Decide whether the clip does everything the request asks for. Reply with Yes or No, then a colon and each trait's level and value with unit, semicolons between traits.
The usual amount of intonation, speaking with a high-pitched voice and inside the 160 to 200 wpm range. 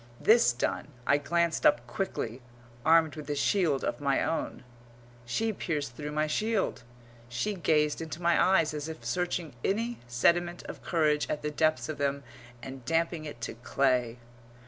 No: average, 3.7 semitones; medium, 155 Hz; average, 165 wpm